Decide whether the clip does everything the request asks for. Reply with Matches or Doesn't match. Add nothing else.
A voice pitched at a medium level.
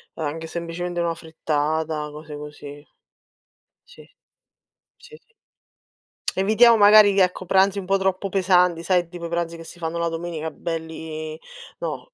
Matches